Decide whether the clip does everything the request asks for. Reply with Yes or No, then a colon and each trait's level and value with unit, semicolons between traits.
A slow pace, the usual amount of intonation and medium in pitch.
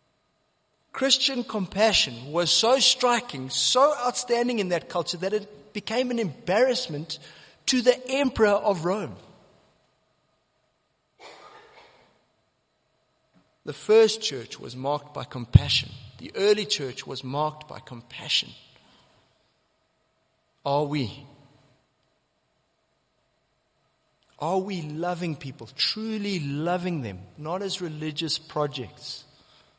No: slow, 95 wpm; wide, 7.5 semitones; medium, 170 Hz